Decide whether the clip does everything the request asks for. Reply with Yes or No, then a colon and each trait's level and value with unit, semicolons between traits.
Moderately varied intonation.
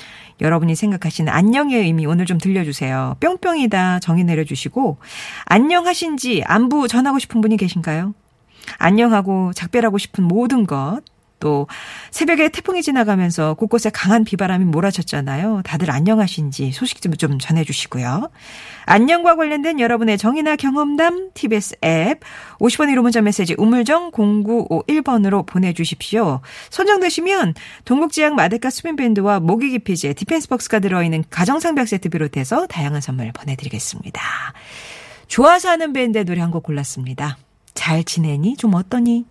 No: wide, 7.5 semitones